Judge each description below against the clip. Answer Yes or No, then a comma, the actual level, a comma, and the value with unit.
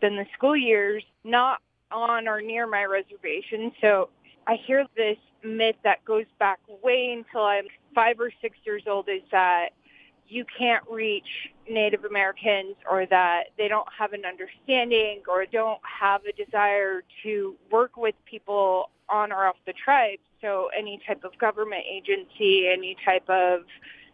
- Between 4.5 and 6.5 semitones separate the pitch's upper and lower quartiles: No, average, 2.7 semitones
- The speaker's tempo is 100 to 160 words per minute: Yes, average, 155 wpm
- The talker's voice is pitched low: No, high, 210 Hz